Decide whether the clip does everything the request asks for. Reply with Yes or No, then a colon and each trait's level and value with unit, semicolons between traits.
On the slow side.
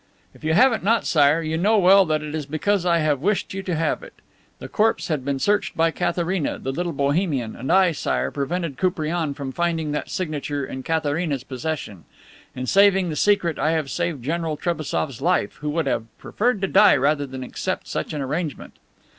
No: average, 200 wpm